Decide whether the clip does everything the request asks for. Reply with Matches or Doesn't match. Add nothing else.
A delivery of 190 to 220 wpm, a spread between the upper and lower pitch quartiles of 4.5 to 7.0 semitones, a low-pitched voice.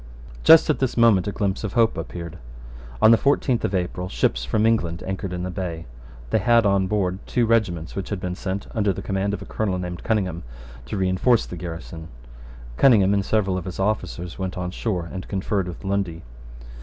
Doesn't match